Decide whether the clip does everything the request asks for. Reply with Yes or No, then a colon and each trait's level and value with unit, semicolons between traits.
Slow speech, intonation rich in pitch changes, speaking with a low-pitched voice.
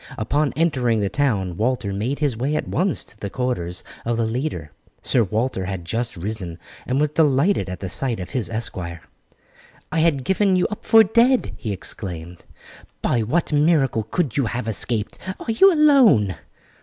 No: average, 175 wpm; wide, 7.1 semitones; low, 120 Hz